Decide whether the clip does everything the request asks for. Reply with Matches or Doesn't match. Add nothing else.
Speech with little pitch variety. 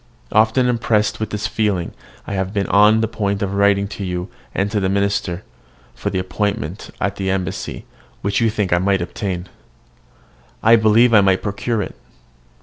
Matches